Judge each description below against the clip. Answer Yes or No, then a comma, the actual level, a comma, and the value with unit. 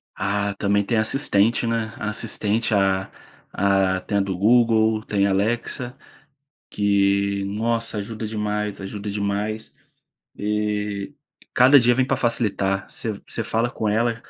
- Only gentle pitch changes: Yes, narrow, 2.3 semitones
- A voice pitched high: No, low, 105 Hz